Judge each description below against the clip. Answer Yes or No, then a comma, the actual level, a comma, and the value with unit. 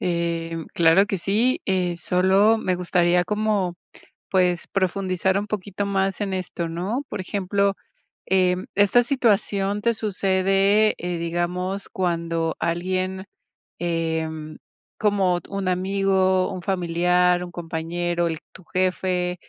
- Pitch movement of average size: No, narrow, 2.1 semitones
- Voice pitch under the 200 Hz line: Yes, medium, 185 Hz